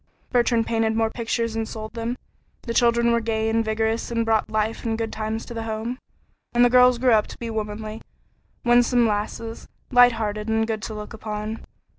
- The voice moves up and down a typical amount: No, narrow, 1.2 semitones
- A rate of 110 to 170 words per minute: No, average, 195 wpm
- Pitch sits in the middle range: No, high, 225 Hz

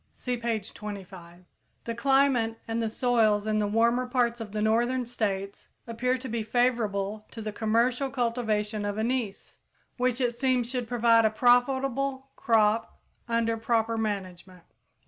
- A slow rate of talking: No, average, 145 wpm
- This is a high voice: Yes, high, 230 Hz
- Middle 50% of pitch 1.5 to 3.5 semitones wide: Yes, narrow, 2.6 semitones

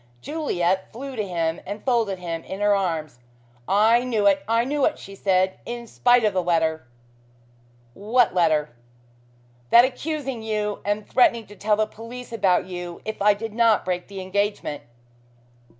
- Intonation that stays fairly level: No, average, 4.5 semitones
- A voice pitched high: Yes, high, 205 Hz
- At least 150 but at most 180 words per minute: Yes, average, 165 wpm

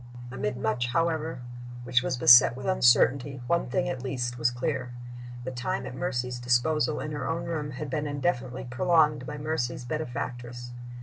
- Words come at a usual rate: Yes, average, 165 wpm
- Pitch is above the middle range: No, low, 130 Hz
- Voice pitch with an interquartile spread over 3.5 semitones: Yes, average, 3.9 semitones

